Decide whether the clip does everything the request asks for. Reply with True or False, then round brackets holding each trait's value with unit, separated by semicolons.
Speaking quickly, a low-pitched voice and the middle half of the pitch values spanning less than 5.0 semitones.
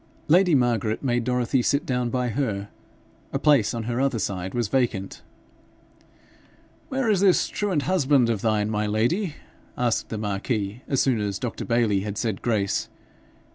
False (160 wpm; 120 Hz; 4.3 semitones)